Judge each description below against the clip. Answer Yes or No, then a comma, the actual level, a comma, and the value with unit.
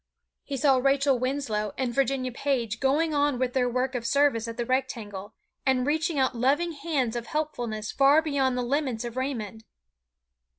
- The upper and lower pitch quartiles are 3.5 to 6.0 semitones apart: No, average, 3.0 semitones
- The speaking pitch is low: No, very high, 260 Hz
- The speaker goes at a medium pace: Yes, average, 170 wpm